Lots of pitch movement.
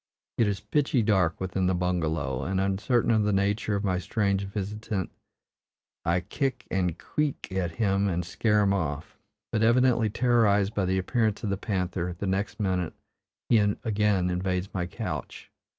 No: average, 2.9 semitones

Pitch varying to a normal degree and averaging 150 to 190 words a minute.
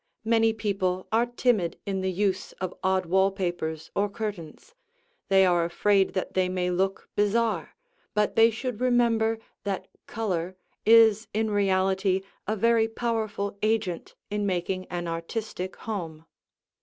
No: average, 3.1 semitones; average, 140 wpm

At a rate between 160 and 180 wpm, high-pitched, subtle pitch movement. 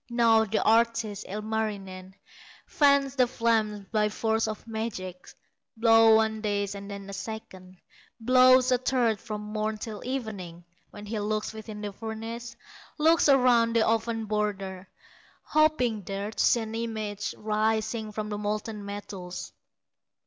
No: average, 140 wpm; high, 220 Hz; narrow, 2.0 semitones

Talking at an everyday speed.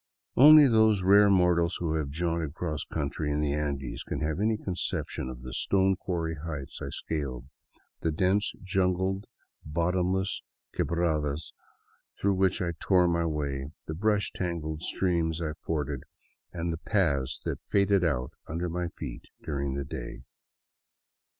Yes: average, 145 wpm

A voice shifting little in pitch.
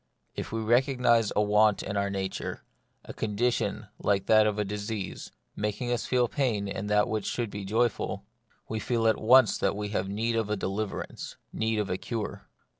Yes: narrow, 2.2 semitones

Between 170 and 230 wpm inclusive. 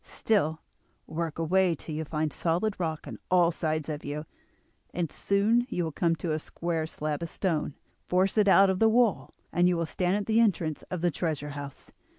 Yes: average, 200 wpm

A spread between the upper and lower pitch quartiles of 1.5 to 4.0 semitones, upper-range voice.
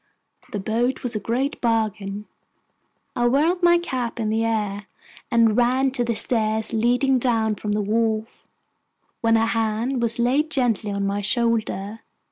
Yes: narrow, 2.4 semitones; high, 230 Hz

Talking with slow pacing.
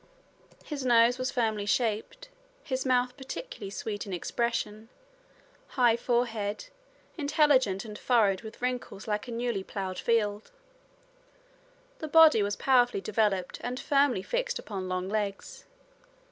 Yes: slow, 125 wpm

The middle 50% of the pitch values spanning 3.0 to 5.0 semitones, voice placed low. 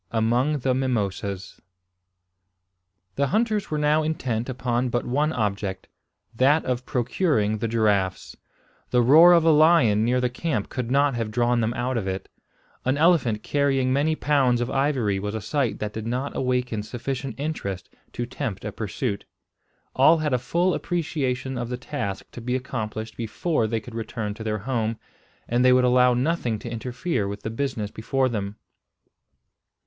Yes: average, 4.0 semitones; low, 125 Hz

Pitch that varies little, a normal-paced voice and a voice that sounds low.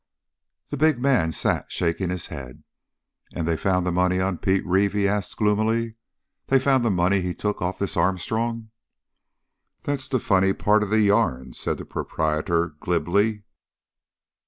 No: average, 3.8 semitones; average, 155 wpm; very low, 95 Hz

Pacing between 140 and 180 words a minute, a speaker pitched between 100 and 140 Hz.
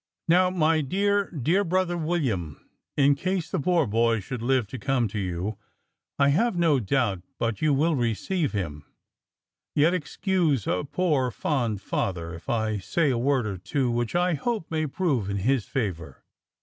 Yes: average, 170 wpm; low, 135 Hz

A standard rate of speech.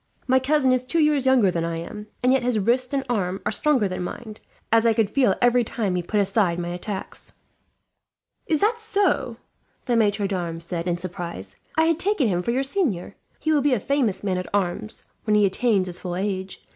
No: fast, 215 wpm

